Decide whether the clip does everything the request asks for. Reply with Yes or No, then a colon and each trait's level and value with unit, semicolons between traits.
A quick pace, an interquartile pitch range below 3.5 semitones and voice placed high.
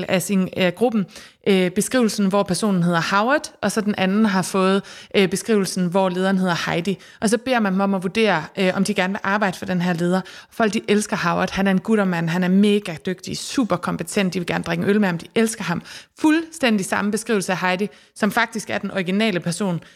Yes: fast, 230 wpm; narrow, 2.6 semitones; high, 195 Hz